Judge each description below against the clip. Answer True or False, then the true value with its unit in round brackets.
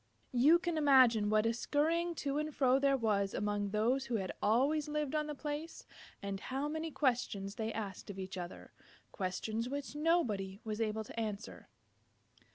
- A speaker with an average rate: True (170 wpm)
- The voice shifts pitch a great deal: True (6.1 semitones)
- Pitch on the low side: False (240 Hz)